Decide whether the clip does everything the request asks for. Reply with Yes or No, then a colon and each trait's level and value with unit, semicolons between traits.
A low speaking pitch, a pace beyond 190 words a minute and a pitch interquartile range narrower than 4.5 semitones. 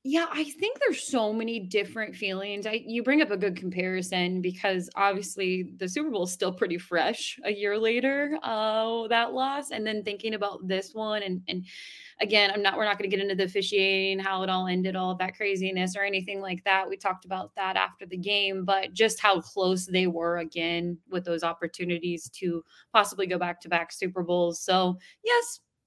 No: high, 195 Hz; average, 200 wpm; average, 2.9 semitones